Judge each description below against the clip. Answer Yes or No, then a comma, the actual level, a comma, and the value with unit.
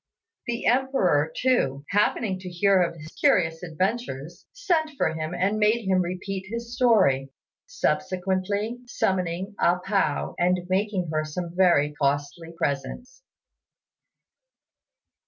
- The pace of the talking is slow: Yes, slow, 120 wpm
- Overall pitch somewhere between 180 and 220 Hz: Yes, medium, 185 Hz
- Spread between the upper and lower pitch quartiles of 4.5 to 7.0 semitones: Yes, average, 4.8 semitones